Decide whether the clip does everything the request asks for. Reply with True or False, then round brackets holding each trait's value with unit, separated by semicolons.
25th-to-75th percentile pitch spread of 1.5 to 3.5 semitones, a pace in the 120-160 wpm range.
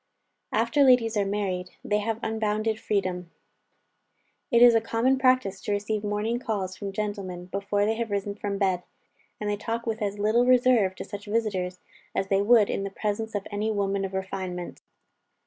False (2.4 semitones; 180 wpm)